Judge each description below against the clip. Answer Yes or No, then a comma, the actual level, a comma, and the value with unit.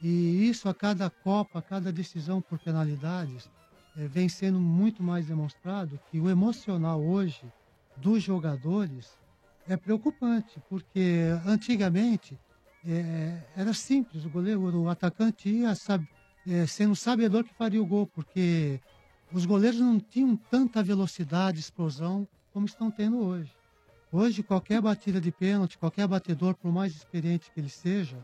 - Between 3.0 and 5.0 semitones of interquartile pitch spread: Yes, average, 3.9 semitones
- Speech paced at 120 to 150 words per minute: Yes, average, 145 wpm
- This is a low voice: No, medium, 185 Hz